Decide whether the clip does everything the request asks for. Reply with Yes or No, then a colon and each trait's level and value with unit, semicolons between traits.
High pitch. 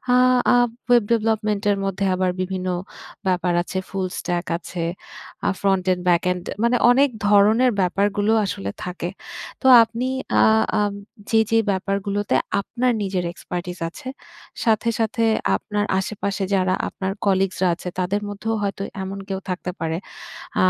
Yes: high, 195 Hz